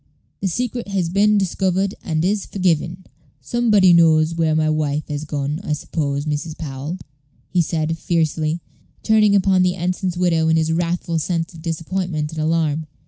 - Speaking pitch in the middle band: Yes, medium, 165 Hz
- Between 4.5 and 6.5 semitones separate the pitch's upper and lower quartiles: No, average, 3.0 semitones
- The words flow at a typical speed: Yes, average, 160 wpm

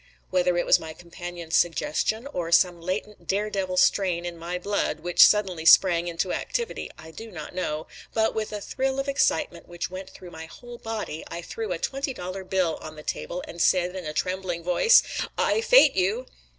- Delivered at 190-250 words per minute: Yes, average, 195 wpm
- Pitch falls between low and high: Yes, medium, 180 Hz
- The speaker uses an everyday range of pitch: Yes, average, 3.5 semitones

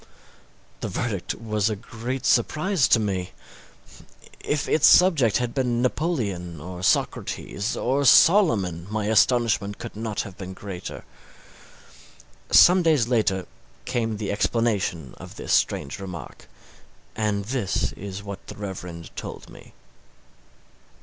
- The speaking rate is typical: No, slow, 125 wpm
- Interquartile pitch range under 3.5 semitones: No, average, 4.3 semitones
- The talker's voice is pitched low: Yes, low, 110 Hz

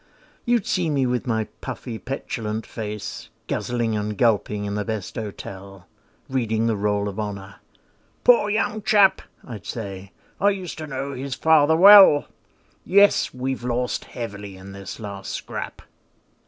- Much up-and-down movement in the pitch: Yes, wide, 5.9 semitones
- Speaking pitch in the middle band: No, low, 115 Hz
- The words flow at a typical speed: Yes, average, 145 wpm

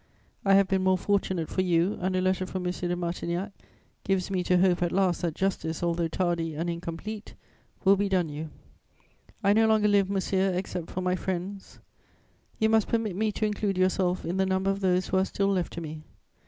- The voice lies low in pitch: No, medium, 185 Hz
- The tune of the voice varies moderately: No, narrow, 2.0 semitones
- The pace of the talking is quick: Yes, fast, 210 wpm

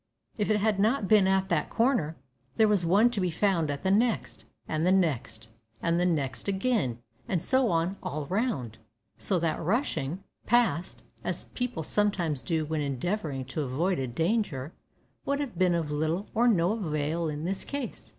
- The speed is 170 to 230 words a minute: Yes, average, 180 wpm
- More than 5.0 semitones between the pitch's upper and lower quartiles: Yes, wide, 5.5 semitones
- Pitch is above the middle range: No, medium, 175 Hz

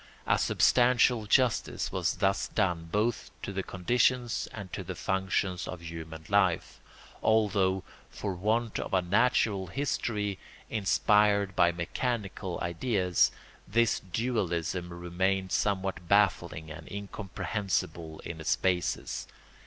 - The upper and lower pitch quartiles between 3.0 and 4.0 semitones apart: Yes, average, 3.3 semitones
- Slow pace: Yes, slow, 115 wpm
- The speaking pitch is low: Yes, very low, 95 Hz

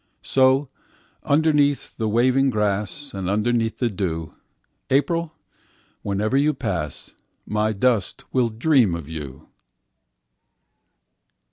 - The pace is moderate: No, slow, 90 wpm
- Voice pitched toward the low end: Yes, low, 115 Hz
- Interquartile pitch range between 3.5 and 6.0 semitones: Yes, wide, 5.4 semitones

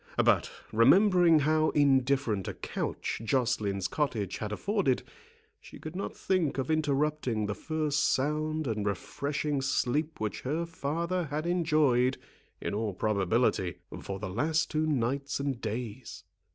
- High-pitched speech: No, medium, 140 Hz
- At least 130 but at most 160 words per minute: Yes, slow, 135 wpm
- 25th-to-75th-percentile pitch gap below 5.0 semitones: No, wide, 5.4 semitones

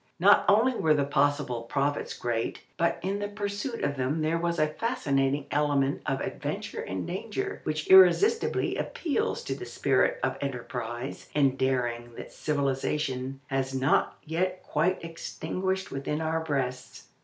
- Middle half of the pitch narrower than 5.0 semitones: No, wide, 5.6 semitones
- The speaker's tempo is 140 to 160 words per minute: Yes, average, 145 wpm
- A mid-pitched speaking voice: Yes, medium, 150 Hz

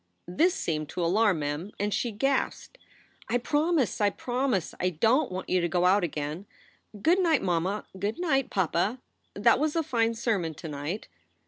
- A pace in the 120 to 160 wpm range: No, average, 185 wpm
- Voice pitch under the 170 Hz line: No, high, 205 Hz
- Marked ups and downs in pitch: Yes, wide, 7.1 semitones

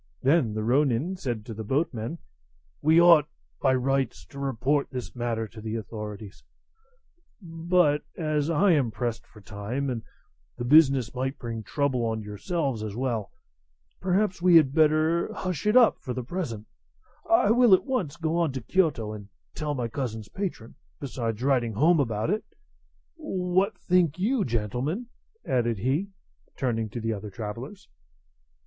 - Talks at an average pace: Yes, average, 155 wpm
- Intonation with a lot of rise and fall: Yes, wide, 6.6 semitones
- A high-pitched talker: No, low, 135 Hz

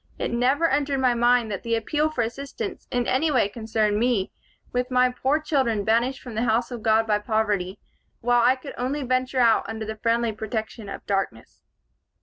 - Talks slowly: No, average, 190 wpm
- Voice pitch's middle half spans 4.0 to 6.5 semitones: No, average, 2.8 semitones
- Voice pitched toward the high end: Yes, high, 235 Hz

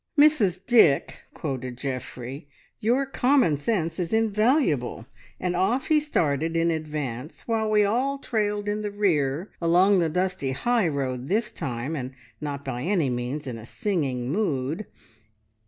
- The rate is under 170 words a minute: Yes, average, 145 wpm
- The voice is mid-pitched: Yes, medium, 165 Hz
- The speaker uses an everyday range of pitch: No, wide, 7.5 semitones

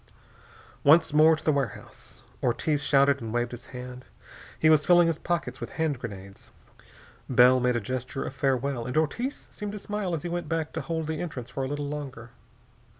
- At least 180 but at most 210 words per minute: Yes, average, 195 wpm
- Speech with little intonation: No, average, 4.3 semitones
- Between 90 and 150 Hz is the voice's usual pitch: Yes, medium, 140 Hz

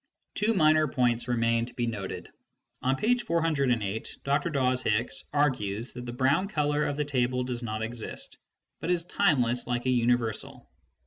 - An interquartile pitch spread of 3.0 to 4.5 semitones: Yes, average, 3.9 semitones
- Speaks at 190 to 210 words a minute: No, average, 165 wpm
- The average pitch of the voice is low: Yes, low, 125 Hz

